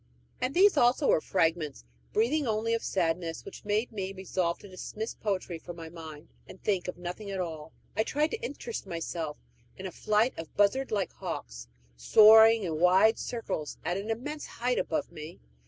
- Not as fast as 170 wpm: No, average, 180 wpm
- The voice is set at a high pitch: Yes, high, 195 Hz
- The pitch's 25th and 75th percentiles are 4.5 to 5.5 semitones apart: Yes, average, 5.1 semitones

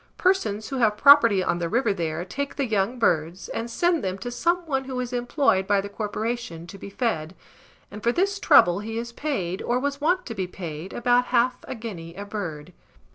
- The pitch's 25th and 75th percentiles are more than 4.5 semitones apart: Yes, average, 5.2 semitones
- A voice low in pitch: No, high, 225 Hz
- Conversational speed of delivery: No, fast, 210 wpm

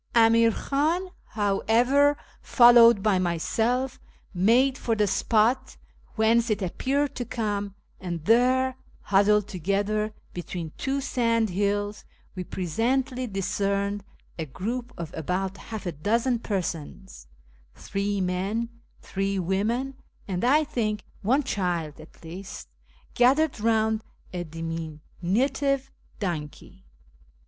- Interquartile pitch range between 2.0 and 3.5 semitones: No, average, 4.6 semitones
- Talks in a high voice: Yes, high, 210 Hz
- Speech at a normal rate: No, slow, 110 wpm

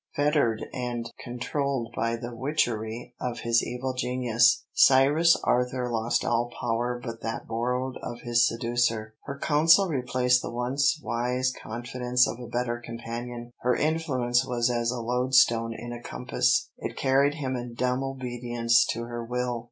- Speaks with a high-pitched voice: No, low, 120 Hz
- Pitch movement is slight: Yes, narrow, 1.5 semitones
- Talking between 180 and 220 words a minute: No, average, 150 wpm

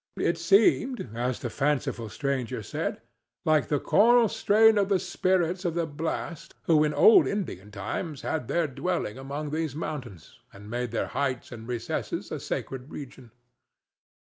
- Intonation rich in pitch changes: Yes, wide, 6.0 semitones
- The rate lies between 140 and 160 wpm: Yes, average, 155 wpm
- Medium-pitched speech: Yes, medium, 150 Hz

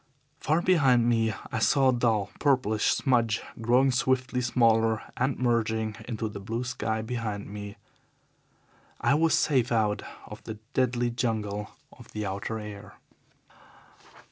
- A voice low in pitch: Yes, low, 115 Hz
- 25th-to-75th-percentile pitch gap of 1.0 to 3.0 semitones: Yes, average, 2.7 semitones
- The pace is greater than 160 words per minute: No, slow, 135 wpm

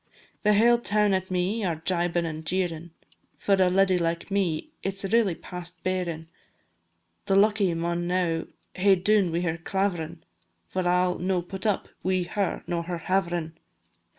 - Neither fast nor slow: Yes, average, 165 wpm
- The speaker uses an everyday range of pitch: No, narrow, 2.3 semitones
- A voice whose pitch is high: No, medium, 180 Hz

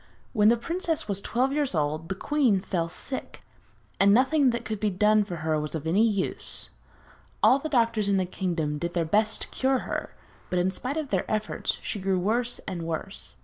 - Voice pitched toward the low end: No, high, 205 Hz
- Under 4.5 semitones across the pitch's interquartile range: No, wide, 5.4 semitones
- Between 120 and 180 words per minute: No, fast, 205 wpm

